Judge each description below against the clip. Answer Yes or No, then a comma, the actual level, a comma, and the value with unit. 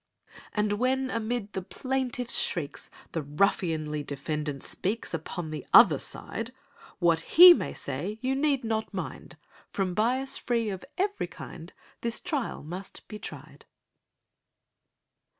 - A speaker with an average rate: No, slow, 130 wpm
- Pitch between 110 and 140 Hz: No, high, 210 Hz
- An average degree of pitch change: No, wide, 7.5 semitones